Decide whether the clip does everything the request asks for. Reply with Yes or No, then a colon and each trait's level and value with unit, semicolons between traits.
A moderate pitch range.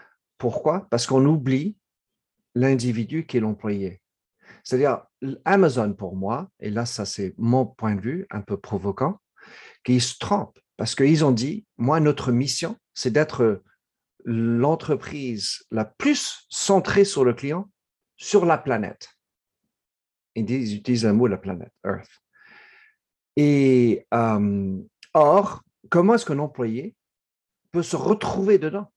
No: wide, 7.3 semitones